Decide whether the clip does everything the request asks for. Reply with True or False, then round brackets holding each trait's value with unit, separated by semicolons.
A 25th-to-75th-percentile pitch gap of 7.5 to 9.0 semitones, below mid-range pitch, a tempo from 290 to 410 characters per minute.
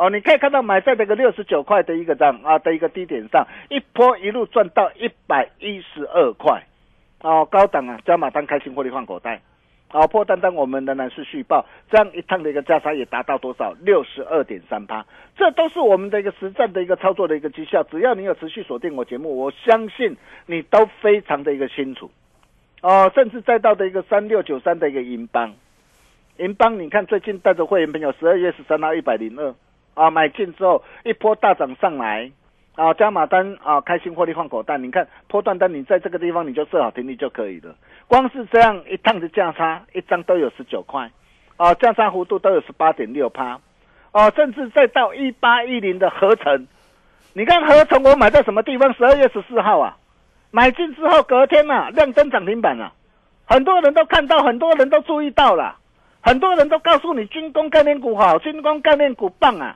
False (7.8 semitones; 200 Hz; 315 characters per minute)